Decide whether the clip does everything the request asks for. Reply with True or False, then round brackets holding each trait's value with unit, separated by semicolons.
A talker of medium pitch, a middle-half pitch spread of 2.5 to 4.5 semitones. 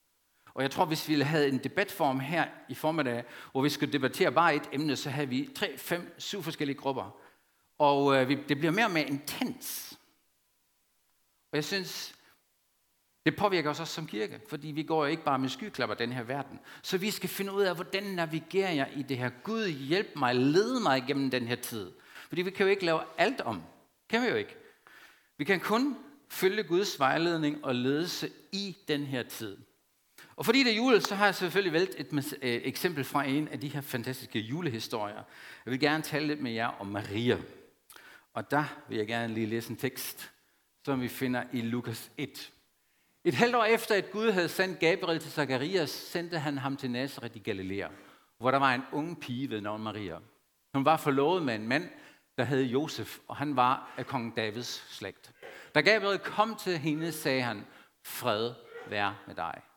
False (145 Hz; 5.3 semitones)